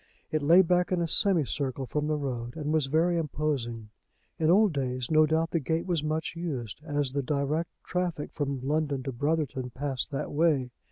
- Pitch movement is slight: No, average, 3.3 semitones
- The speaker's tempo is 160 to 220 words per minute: Yes, average, 190 wpm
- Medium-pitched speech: Yes, medium, 150 Hz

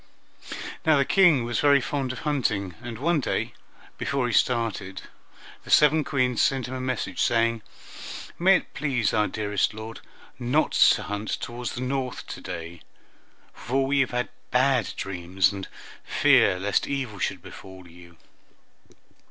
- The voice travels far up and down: No, average, 5.0 semitones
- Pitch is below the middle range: Yes, low, 120 Hz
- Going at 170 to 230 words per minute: No, average, 150 wpm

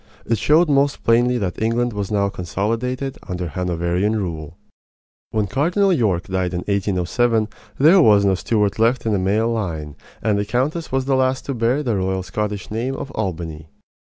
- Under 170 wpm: No, average, 175 wpm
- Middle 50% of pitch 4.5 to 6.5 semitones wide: Yes, average, 5.1 semitones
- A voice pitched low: Yes, low, 110 Hz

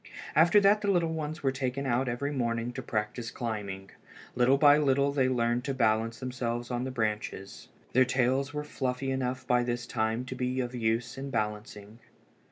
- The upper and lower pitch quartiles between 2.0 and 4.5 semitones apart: Yes, narrow, 2.6 semitones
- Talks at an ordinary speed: Yes, average, 180 wpm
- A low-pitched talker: Yes, low, 125 Hz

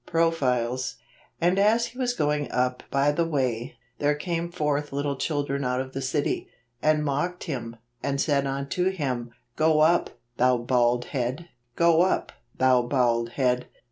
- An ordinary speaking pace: Yes, average, 160 wpm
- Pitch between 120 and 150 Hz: Yes, medium, 140 Hz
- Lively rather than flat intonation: No, average, 4.5 semitones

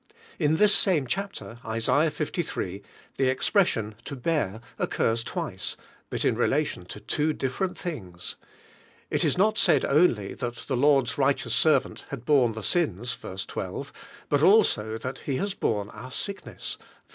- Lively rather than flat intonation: Yes, wide, 5.9 semitones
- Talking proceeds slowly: No, average, 165 wpm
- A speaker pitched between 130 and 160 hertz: Yes, low, 135 Hz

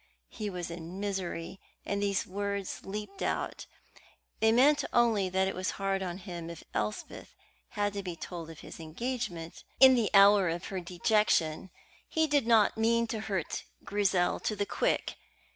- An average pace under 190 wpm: Yes, average, 165 wpm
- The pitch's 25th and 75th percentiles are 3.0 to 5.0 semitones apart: Yes, average, 3.4 semitones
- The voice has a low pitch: No, high, 195 Hz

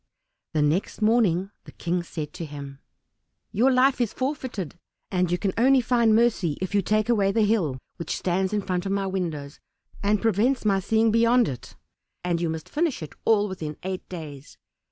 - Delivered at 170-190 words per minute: Yes, average, 185 wpm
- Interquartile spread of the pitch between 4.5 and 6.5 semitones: Yes, average, 4.9 semitones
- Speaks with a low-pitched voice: No, high, 195 Hz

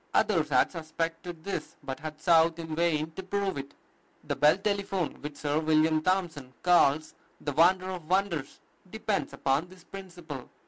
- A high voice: No, medium, 165 Hz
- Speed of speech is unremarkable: Yes, average, 155 wpm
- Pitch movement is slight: No, average, 3.2 semitones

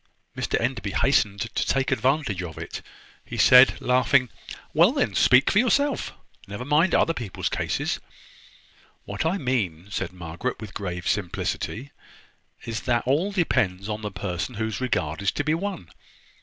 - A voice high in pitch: No, low, 115 Hz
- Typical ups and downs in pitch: No, wide, 6.2 semitones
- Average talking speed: Yes, average, 155 wpm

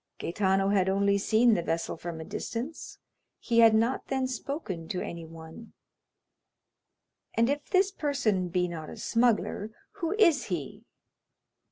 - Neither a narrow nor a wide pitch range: No, wide, 6.5 semitones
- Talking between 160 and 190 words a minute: No, average, 140 wpm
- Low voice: No, high, 210 Hz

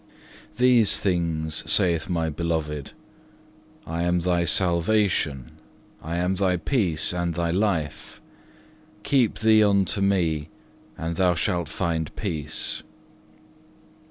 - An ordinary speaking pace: No, slow, 110 wpm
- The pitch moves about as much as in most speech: Yes, average, 3.2 semitones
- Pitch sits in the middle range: No, very low, 85 Hz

